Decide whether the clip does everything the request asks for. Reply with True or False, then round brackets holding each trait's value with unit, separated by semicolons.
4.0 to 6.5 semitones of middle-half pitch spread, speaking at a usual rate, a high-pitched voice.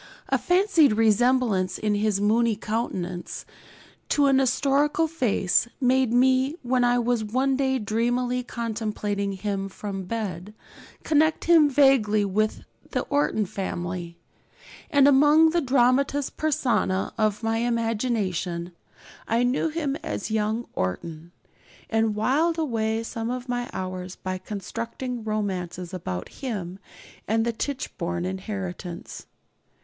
False (4.9 semitones; 120 wpm; 225 Hz)